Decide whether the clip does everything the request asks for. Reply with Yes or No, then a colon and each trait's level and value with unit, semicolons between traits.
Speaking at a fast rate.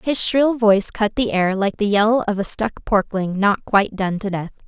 Yes: fast, 230 wpm